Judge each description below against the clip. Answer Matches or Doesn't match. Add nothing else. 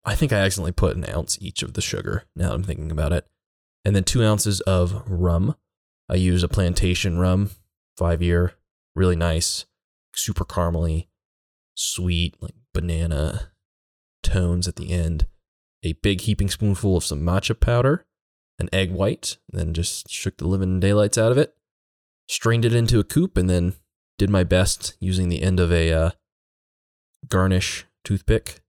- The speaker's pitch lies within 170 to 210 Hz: Doesn't match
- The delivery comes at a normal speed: Matches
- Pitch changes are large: Doesn't match